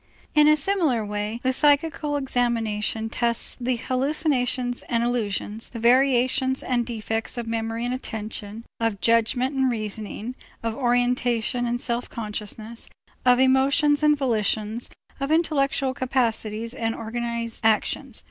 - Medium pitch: No, high, 240 Hz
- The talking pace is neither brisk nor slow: No, slow, 130 wpm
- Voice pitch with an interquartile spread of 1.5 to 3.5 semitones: Yes, average, 2.7 semitones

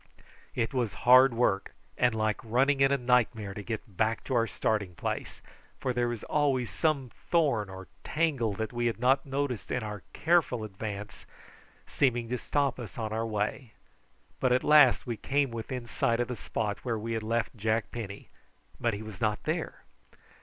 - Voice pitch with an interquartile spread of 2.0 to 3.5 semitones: Yes, average, 2.9 semitones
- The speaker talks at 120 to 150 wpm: No, average, 180 wpm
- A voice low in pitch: Yes, low, 115 Hz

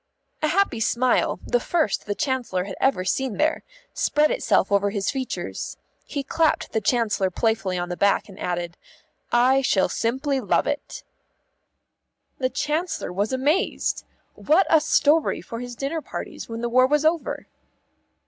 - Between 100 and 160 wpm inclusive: Yes, average, 155 wpm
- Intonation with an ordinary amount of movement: No, wide, 6.6 semitones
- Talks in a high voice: Yes, very high, 255 Hz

